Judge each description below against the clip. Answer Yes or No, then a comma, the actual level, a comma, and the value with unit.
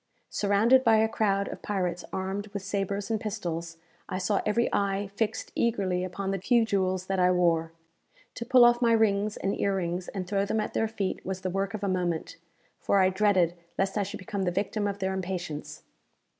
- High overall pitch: Yes, high, 195 Hz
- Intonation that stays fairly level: Yes, narrow, 2.3 semitones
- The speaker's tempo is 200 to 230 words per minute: Yes, fast, 205 wpm